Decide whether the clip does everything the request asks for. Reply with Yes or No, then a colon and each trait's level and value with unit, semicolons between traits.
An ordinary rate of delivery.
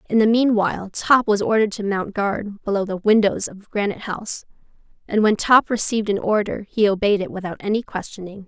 Yes: average, 190 wpm